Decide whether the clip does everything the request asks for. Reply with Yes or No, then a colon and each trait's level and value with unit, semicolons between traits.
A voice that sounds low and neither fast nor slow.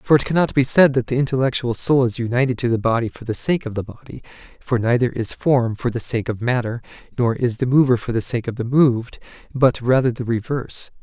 No: low, 125 Hz; fast, 235 wpm